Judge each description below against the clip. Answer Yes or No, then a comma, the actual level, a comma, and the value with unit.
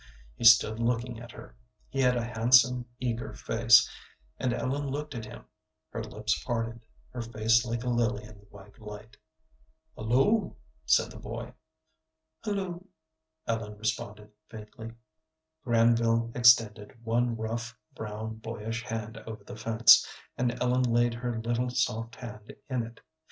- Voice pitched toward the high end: No, low, 115 Hz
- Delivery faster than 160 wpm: No, average, 140 wpm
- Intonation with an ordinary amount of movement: No, narrow, 1.8 semitones